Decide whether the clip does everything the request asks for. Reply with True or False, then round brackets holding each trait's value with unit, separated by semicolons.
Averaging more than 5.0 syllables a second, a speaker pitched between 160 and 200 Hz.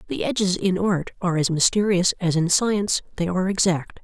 True (5.6 syllables/s; 185 Hz)